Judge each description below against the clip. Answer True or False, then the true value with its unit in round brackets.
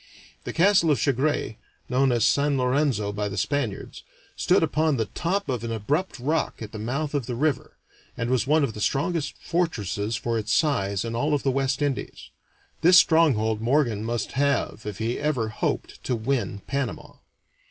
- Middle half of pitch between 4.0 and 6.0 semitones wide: True (4.7 semitones)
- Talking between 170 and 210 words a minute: True (180 wpm)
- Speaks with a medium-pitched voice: False (130 Hz)